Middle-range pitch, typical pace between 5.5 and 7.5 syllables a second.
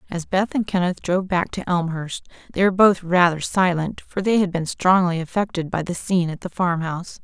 Yes: medium, 180 Hz; 5.6 syllables/s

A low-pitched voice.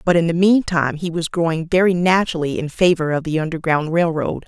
No: medium, 165 Hz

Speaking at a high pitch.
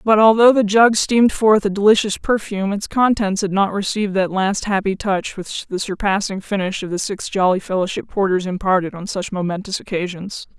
Yes: high, 200 Hz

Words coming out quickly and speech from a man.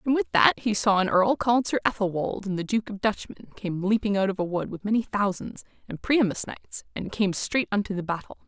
No: fast, 235 wpm; female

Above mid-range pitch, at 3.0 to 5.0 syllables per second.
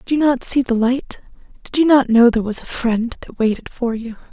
No: high, 245 Hz; 5.5 syllables/s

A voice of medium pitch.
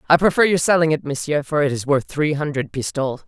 Yes: medium, 150 Hz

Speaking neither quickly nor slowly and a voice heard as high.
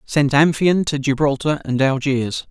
No: average, 145 wpm; medium, 140 Hz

